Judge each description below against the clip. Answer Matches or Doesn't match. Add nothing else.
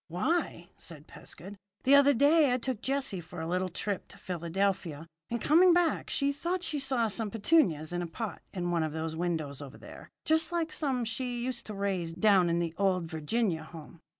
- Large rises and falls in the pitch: Matches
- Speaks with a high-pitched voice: Matches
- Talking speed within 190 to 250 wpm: Matches